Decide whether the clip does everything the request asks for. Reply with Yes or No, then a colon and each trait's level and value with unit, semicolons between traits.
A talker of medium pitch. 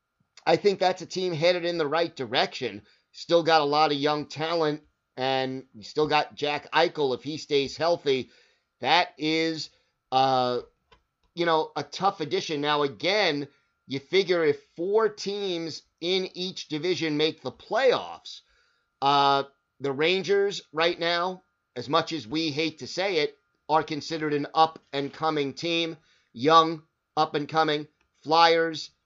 Yes: medium, 155 Hz